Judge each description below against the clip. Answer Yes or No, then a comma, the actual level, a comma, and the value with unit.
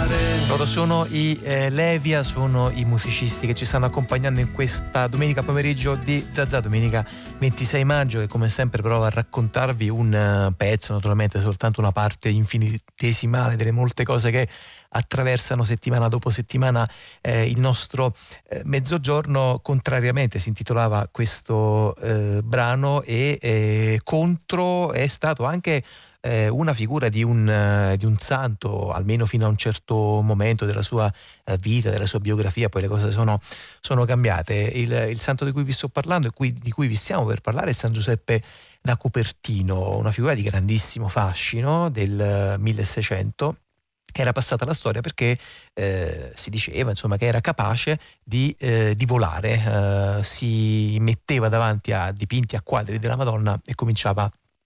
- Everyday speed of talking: Yes, average, 155 wpm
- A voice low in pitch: Yes, low, 115 Hz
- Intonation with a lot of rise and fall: No, average, 3.4 semitones